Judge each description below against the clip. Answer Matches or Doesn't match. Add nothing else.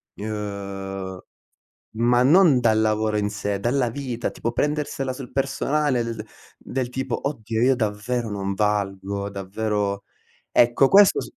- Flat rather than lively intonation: Doesn't match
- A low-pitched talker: Matches